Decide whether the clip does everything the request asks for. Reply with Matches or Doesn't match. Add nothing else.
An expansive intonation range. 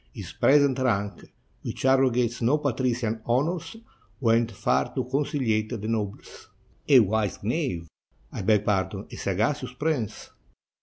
Doesn't match